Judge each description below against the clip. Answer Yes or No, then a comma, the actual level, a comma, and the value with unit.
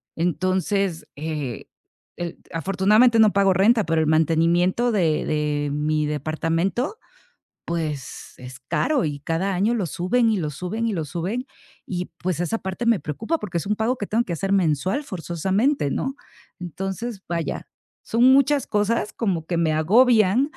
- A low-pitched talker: No, medium, 185 Hz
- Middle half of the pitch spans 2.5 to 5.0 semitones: No, wide, 5.4 semitones